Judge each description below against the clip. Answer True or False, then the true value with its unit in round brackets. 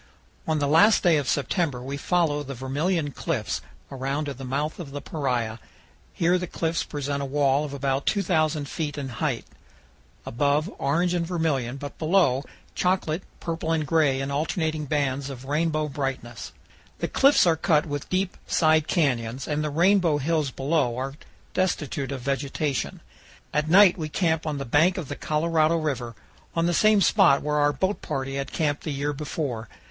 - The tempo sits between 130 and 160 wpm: False (175 wpm)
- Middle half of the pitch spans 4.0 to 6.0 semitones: False (3.1 semitones)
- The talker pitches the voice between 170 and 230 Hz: False (150 Hz)